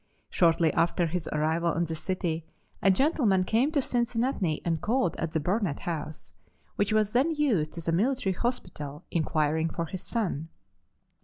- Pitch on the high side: No, medium, 175 Hz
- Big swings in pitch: Yes, wide, 5.9 semitones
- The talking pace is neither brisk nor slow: Yes, average, 160 wpm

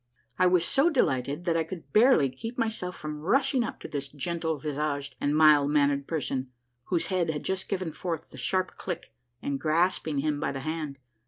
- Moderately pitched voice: Yes, medium, 155 Hz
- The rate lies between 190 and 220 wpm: Yes, average, 195 wpm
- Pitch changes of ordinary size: Yes, average, 4.3 semitones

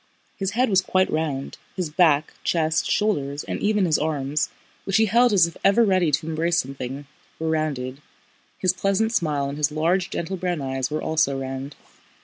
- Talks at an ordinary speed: Yes, average, 180 wpm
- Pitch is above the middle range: No, medium, 160 Hz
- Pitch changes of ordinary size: Yes, average, 4.7 semitones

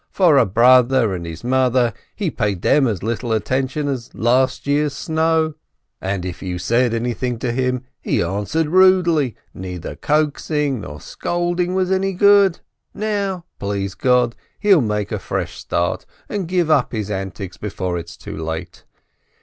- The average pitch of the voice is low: Yes, low, 125 Hz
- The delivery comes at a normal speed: Yes, average, 160 wpm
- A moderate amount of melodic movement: No, wide, 7.9 semitones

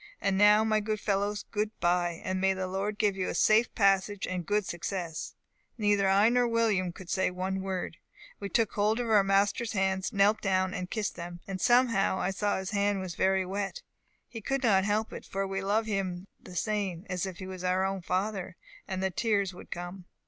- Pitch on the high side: Yes, high, 195 Hz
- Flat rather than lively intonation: Yes, narrow, 2.0 semitones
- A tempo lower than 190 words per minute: No, fast, 205 wpm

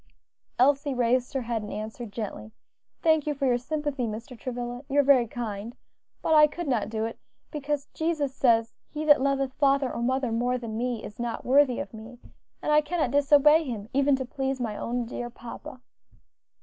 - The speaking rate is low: No, average, 190 wpm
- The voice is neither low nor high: No, very high, 255 Hz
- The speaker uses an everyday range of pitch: Yes, average, 3.4 semitones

